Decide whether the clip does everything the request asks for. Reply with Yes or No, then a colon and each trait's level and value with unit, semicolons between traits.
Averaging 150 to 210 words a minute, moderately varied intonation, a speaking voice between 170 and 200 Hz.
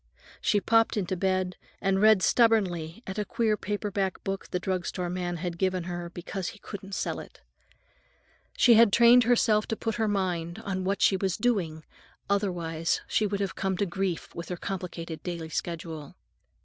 Yes: average, 175 wpm; average, 3.0 semitones; high, 190 Hz